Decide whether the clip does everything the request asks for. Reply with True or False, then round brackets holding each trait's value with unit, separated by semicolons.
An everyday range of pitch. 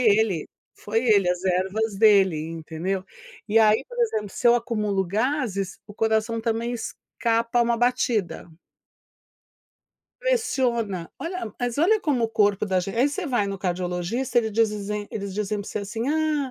True (3.6 semitones)